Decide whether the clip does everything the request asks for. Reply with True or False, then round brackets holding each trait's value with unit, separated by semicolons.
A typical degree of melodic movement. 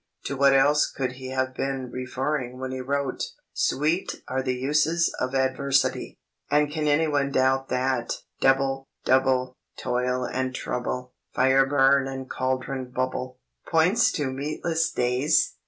False (1.6 semitones)